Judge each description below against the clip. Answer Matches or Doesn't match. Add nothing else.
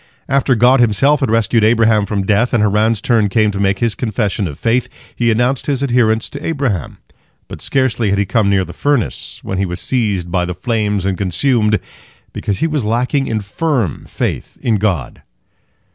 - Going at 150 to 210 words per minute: Matches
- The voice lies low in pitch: Matches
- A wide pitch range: Doesn't match